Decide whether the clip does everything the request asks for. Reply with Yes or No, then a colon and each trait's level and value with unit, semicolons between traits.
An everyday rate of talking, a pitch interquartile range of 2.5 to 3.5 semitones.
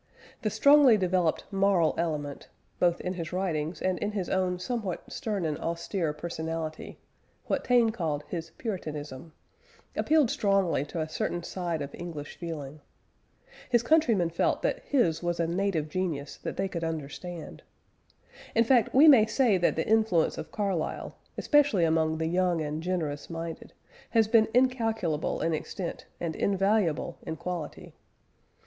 No: average, 150 wpm; average, 4.7 semitones